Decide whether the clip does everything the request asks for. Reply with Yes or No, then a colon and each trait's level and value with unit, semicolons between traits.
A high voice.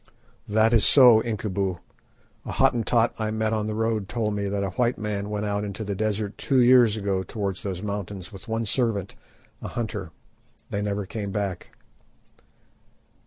No: low, 105 Hz